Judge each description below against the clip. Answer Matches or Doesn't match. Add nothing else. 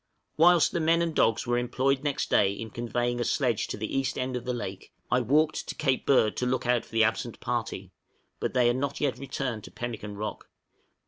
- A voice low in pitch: Matches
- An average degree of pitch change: Matches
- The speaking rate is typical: Doesn't match